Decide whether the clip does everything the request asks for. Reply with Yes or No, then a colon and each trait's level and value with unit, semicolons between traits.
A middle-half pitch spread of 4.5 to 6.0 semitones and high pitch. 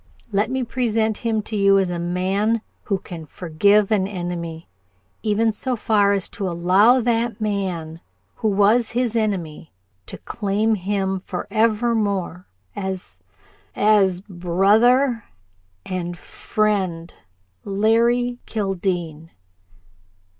No: average, 3.4 semitones; high, 200 Hz